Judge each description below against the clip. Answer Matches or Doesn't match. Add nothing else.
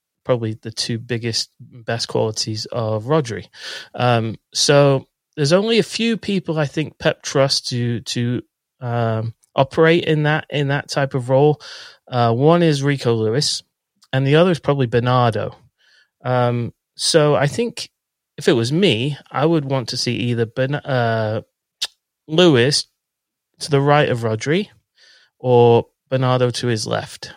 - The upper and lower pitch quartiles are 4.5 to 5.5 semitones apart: Doesn't match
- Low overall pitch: Matches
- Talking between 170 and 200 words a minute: Doesn't match